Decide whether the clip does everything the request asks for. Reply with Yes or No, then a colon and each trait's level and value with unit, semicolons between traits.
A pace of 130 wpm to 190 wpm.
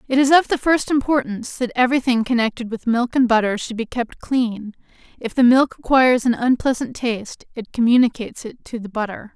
No: average, 200 wpm